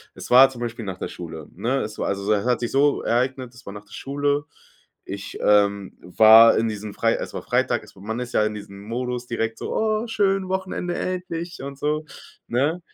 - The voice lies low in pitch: Yes, low, 120 Hz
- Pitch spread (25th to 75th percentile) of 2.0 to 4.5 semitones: No, wide, 5.5 semitones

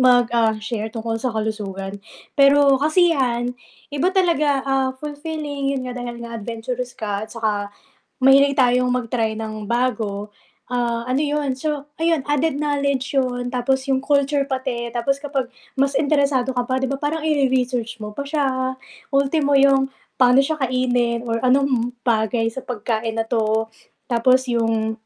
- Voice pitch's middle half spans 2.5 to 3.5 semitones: Yes, average, 3.1 semitones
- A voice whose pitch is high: Yes, very high, 255 Hz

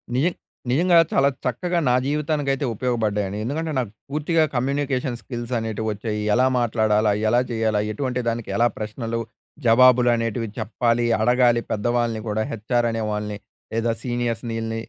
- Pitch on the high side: No, low, 120 Hz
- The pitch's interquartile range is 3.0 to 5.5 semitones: No, narrow, 2.5 semitones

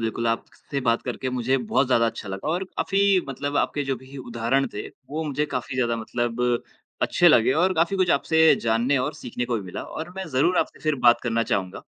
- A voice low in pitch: Yes, low, 130 Hz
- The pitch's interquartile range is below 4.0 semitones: No, average, 4.7 semitones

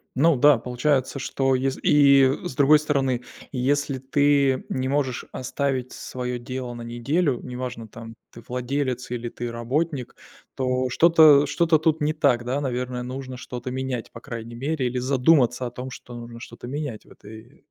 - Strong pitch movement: No, narrow, 2.5 semitones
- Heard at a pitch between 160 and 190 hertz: No, low, 130 Hz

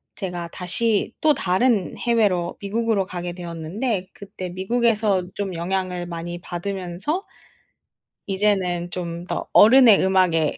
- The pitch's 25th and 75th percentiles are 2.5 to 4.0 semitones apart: Yes, average, 3.2 semitones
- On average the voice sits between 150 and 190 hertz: Yes, medium, 185 Hz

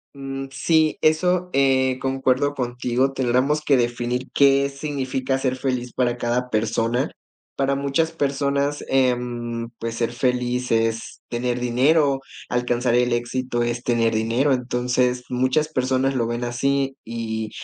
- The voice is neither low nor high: No, low, 125 Hz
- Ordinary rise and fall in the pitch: No, narrow, 2.2 semitones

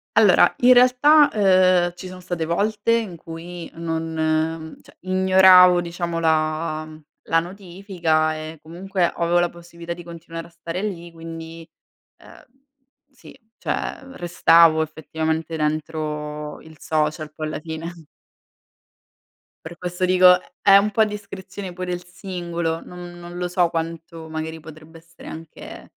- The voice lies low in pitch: No, medium, 170 Hz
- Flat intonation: Yes, narrow, 2.3 semitones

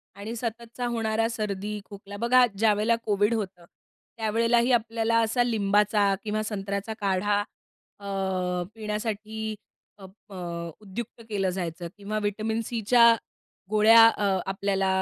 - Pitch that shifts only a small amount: Yes, narrow, 2.1 semitones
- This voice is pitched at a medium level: No, high, 215 Hz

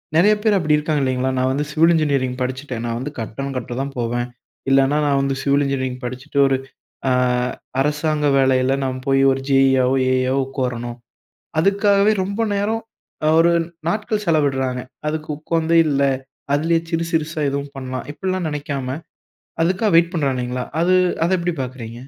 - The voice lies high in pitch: No, medium, 140 Hz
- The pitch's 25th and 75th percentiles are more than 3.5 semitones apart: Yes, average, 4.0 semitones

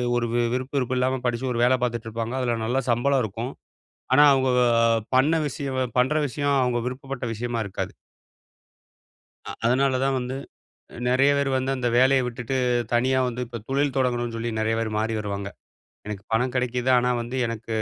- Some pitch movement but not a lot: No, narrow, 2.0 semitones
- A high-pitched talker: No, low, 125 Hz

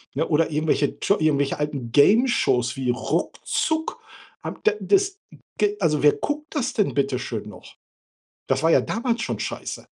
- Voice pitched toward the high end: No, medium, 160 Hz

